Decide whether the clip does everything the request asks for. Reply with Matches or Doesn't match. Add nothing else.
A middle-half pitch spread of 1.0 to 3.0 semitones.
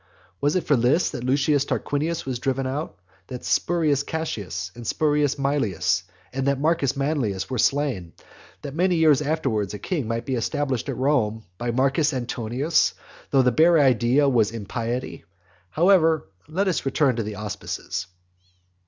Doesn't match